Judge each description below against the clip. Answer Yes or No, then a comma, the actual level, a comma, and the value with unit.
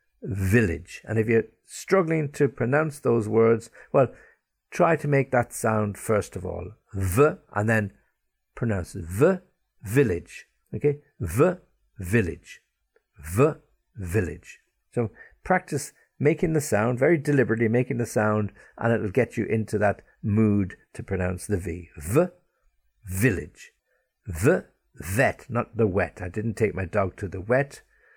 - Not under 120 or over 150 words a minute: Yes, average, 140 wpm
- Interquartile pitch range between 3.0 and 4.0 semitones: No, wide, 5.6 semitones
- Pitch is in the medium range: No, low, 115 Hz